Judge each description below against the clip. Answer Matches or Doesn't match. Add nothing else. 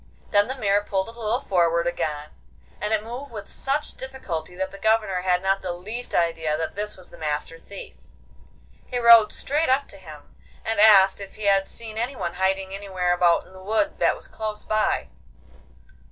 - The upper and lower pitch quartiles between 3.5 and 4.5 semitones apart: Matches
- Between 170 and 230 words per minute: Matches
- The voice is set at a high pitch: Matches